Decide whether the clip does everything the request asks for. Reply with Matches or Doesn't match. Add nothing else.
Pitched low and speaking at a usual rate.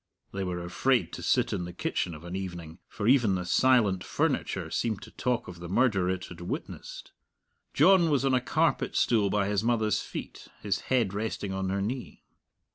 Matches